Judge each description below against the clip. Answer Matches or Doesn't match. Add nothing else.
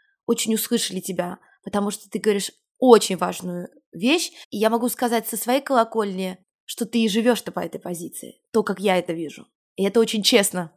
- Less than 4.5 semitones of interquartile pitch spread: Matches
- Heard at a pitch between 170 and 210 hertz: Doesn't match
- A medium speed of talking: Doesn't match